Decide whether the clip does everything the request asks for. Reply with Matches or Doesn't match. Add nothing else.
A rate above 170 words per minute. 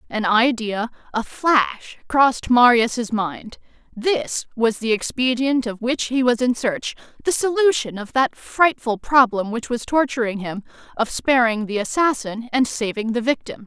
Doesn't match